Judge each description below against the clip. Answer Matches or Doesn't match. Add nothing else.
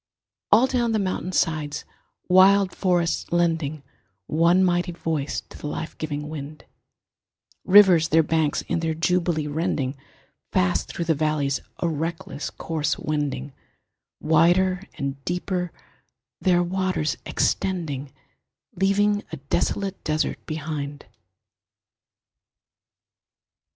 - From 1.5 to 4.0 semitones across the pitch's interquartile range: Matches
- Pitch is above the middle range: Doesn't match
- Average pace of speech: Doesn't match